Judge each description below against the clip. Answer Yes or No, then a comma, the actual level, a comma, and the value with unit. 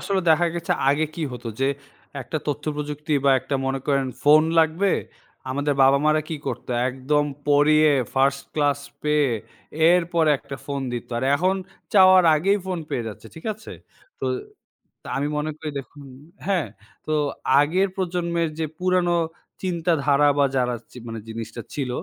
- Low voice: No, medium, 150 Hz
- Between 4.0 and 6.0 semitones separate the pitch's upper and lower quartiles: No, average, 3.6 semitones